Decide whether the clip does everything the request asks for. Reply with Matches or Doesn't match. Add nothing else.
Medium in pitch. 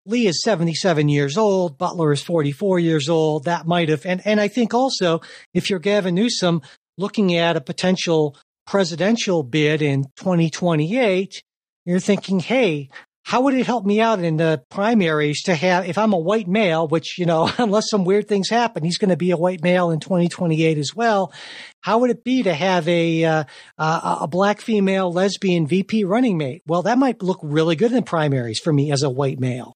Matches